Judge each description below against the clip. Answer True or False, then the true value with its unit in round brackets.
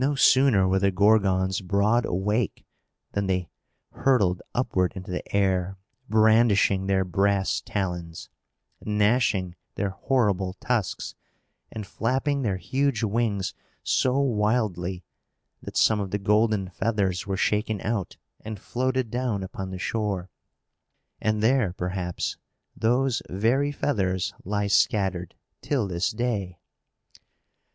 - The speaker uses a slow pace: True (120 wpm)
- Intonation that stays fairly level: False (3.4 semitones)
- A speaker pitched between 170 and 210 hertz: False (100 Hz)